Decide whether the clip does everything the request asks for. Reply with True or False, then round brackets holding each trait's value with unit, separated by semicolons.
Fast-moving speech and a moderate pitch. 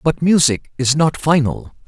False (160 wpm; 145 Hz)